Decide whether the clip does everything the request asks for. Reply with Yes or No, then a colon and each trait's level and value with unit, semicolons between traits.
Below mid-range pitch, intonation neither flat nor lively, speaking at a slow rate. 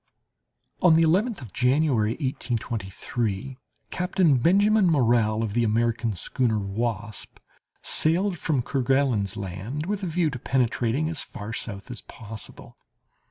No: low, 125 Hz; wide, 6.2 semitones; slow, 125 wpm